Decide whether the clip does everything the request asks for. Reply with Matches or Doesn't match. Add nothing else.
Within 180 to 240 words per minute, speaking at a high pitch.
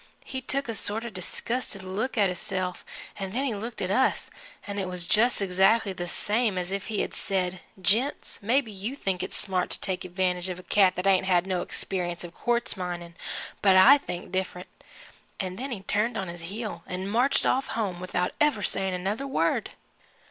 Matches